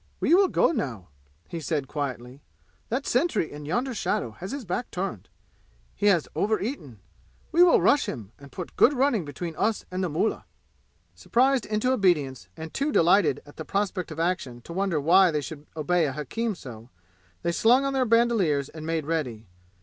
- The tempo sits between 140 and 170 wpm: No, average, 185 wpm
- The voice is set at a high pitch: No, medium, 175 Hz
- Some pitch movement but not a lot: No, wide, 7.8 semitones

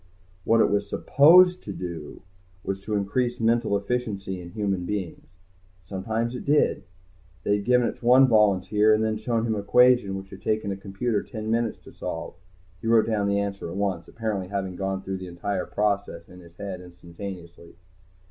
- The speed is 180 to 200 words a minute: Yes, average, 185 wpm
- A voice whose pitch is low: Yes, low, 100 Hz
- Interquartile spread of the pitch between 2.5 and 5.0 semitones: Yes, average, 2.9 semitones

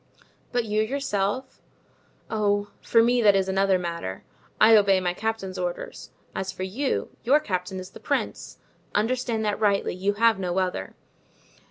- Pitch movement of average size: Yes, average, 3.3 semitones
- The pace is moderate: Yes, average, 155 wpm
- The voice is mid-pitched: No, high, 205 Hz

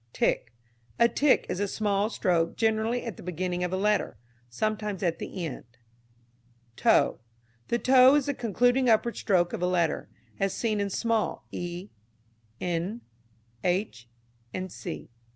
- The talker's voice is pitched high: Yes, high, 200 Hz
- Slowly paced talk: No, average, 145 wpm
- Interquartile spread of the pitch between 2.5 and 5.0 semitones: Yes, average, 4.5 semitones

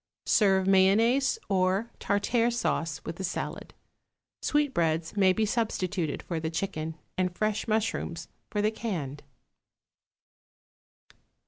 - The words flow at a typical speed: No, slow, 110 wpm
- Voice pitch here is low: No, high, 195 Hz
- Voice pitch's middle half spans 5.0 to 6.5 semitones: No, average, 4.5 semitones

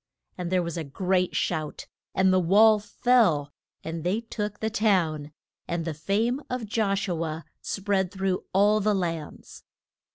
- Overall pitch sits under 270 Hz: Yes, high, 190 Hz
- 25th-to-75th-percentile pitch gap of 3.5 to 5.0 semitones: Yes, average, 3.9 semitones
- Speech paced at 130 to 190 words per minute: Yes, average, 160 wpm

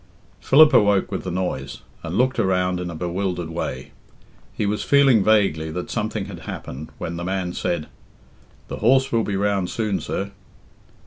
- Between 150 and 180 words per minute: Yes, average, 170 wpm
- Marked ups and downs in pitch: No, average, 3.4 semitones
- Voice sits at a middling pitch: No, very low, 95 Hz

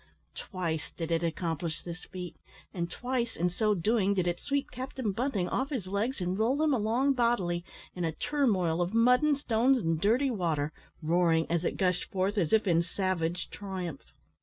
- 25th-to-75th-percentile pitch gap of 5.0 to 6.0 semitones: Yes, wide, 5.6 semitones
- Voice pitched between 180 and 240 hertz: Yes, medium, 185 Hz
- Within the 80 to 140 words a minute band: No, average, 185 wpm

